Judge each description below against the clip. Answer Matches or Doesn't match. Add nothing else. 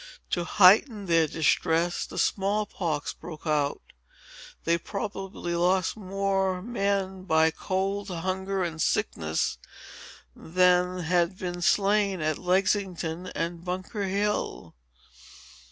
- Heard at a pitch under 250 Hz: Matches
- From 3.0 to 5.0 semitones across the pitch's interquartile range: Doesn't match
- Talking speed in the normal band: Doesn't match